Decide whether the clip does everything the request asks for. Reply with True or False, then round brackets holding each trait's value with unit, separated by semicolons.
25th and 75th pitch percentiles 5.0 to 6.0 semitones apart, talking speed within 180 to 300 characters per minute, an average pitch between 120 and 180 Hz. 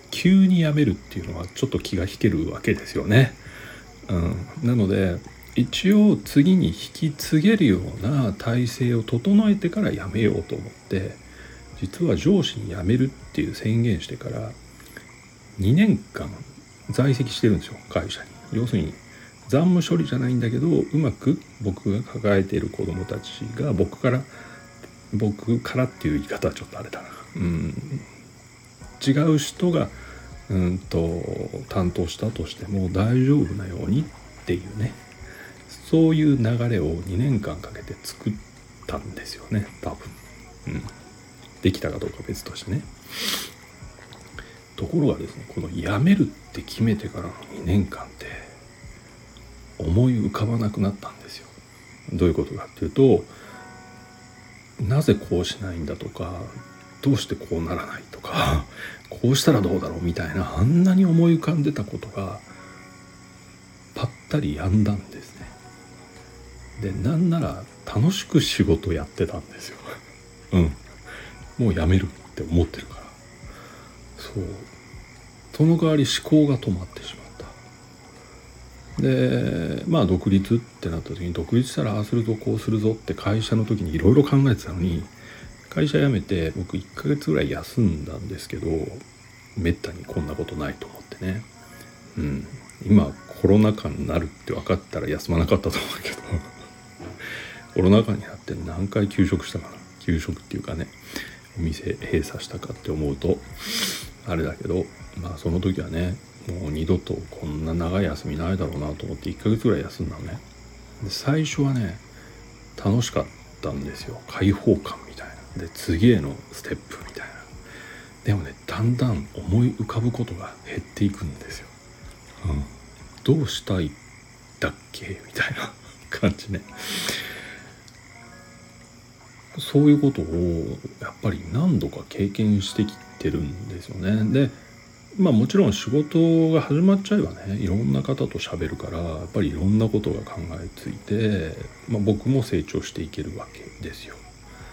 False (5.4 semitones; 295 characters per minute; 105 Hz)